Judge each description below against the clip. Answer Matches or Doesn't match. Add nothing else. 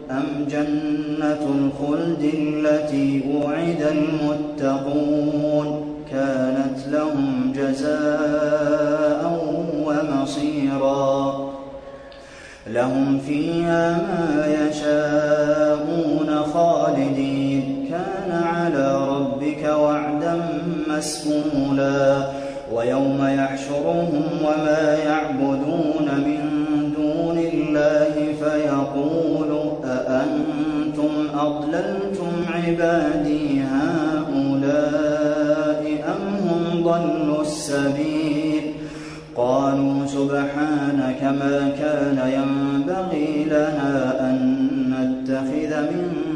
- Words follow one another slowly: Matches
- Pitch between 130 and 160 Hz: Matches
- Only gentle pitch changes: Matches